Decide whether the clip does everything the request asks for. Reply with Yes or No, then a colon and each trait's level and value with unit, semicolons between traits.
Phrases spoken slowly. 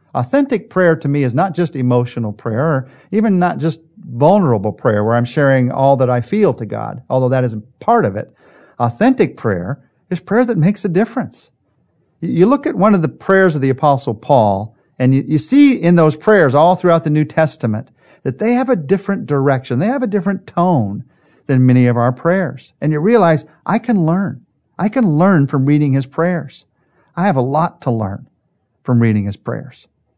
No: average, 200 wpm